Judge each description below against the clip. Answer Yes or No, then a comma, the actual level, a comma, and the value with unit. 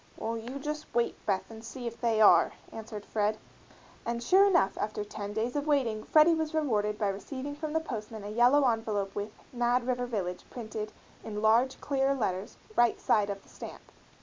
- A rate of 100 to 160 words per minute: No, average, 190 wpm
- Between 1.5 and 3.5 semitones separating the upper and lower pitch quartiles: No, average, 4.1 semitones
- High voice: Yes, high, 230 Hz